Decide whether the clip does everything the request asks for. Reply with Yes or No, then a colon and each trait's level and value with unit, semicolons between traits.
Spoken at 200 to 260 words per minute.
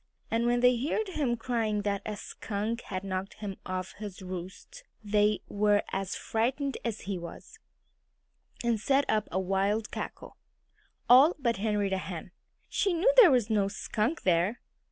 No: average, 155 wpm